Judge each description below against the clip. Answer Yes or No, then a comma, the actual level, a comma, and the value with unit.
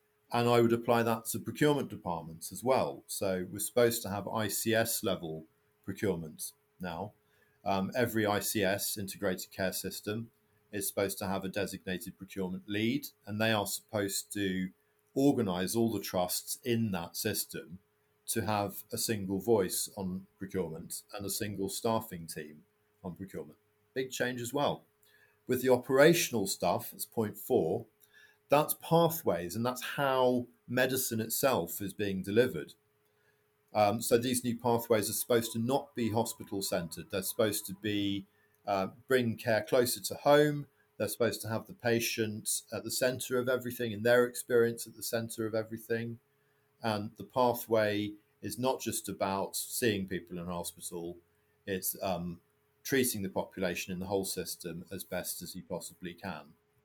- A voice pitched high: No, low, 110 Hz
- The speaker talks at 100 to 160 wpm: Yes, average, 155 wpm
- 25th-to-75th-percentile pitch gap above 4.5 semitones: No, average, 3.6 semitones